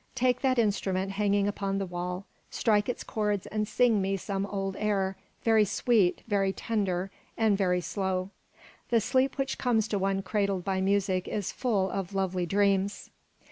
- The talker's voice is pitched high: Yes, high, 200 Hz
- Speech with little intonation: Yes, narrow, 1.9 semitones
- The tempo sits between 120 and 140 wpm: No, average, 165 wpm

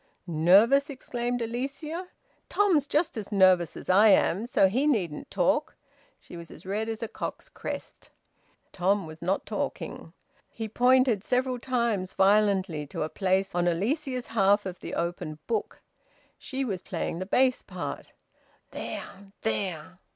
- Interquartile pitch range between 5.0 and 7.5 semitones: Yes, average, 5.3 semitones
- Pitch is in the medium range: No, high, 205 Hz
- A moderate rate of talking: Yes, average, 145 wpm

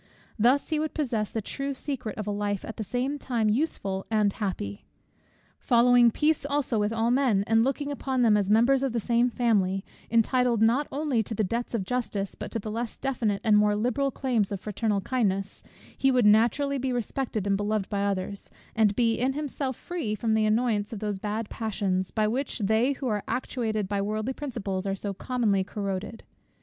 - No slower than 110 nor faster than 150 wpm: No, average, 195 wpm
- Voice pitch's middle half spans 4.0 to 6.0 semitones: No, average, 3.6 semitones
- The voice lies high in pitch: Yes, high, 225 Hz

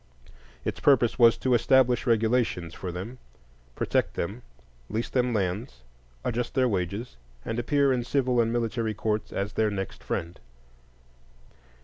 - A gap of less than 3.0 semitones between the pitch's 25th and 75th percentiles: No, average, 3.6 semitones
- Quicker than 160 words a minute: No, slow, 135 wpm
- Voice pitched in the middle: No, low, 115 Hz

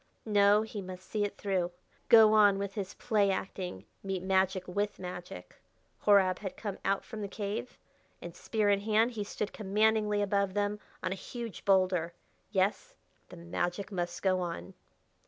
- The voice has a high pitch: Yes, high, 200 Hz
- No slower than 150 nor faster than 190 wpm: Yes, average, 165 wpm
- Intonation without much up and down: Yes, narrow, 2.1 semitones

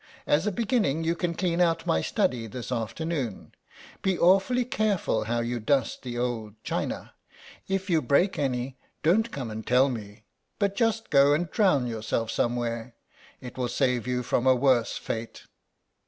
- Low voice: Yes, low, 130 Hz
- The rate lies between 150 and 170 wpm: Yes, average, 165 wpm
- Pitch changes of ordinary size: No, wide, 6.8 semitones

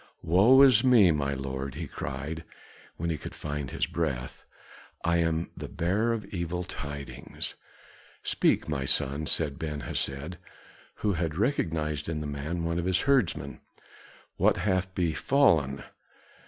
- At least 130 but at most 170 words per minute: Yes, average, 140 wpm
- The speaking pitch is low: Yes, very low, 80 Hz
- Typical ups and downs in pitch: Yes, average, 4.5 semitones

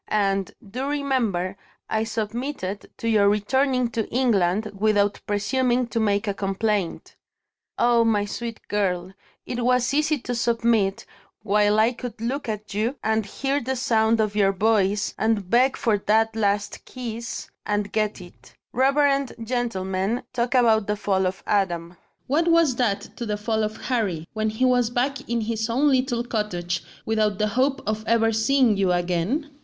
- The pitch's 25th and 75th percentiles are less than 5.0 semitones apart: Yes, average, 3.3 semitones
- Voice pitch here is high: Yes, high, 220 Hz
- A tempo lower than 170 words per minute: Yes, average, 160 wpm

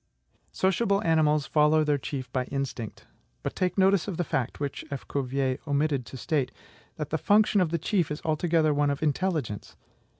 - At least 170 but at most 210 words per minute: Yes, average, 175 wpm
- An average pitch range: Yes, average, 3.6 semitones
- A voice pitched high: No, medium, 150 Hz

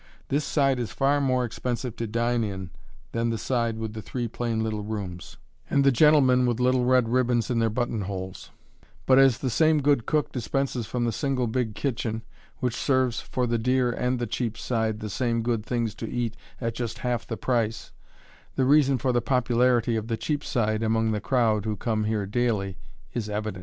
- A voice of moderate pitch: No, low, 120 Hz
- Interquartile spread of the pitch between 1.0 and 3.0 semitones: Yes, narrow, 2.5 semitones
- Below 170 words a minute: No, average, 200 wpm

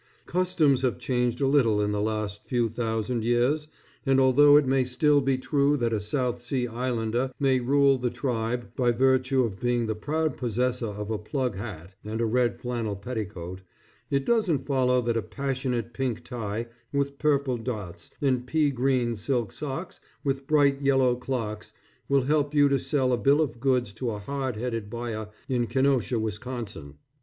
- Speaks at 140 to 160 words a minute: No, average, 175 wpm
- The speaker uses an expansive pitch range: No, average, 3.2 semitones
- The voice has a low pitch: Yes, low, 125 Hz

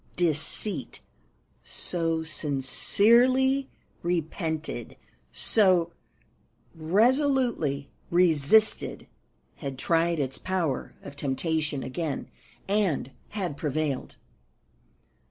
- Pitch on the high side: No, medium, 165 Hz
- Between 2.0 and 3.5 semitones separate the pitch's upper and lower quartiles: No, wide, 5.6 semitones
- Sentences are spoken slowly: Yes, slow, 65 wpm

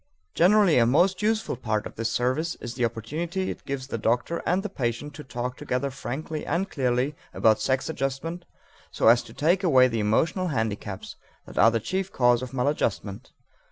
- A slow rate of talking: No, average, 185 wpm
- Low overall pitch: Yes, low, 130 Hz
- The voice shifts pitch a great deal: Yes, wide, 5.9 semitones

